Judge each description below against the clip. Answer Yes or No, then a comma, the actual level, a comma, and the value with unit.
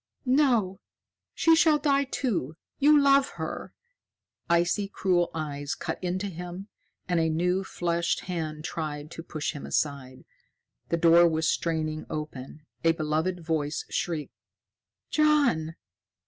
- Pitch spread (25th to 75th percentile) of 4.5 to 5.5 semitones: No, average, 4.1 semitones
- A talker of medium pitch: Yes, medium, 170 Hz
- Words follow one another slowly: Yes, slow, 125 wpm